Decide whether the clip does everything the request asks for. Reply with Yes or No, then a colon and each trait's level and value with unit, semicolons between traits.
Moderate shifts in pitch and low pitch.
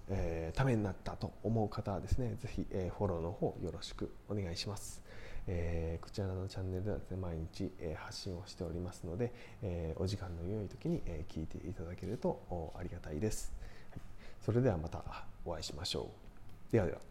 Yes: average, 3.2 semitones; very low, 95 Hz